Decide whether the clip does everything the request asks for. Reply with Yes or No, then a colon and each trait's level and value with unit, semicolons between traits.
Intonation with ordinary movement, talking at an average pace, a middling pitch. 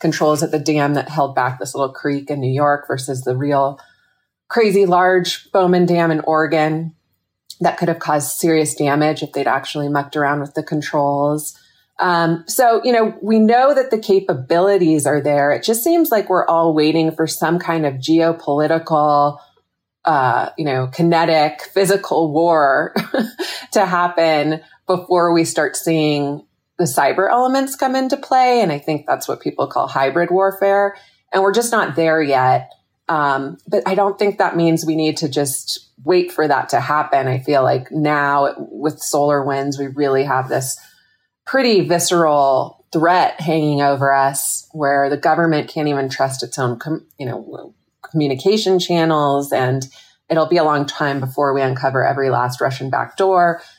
Yes: average, 4.2 semitones; average, 170 wpm; medium, 155 Hz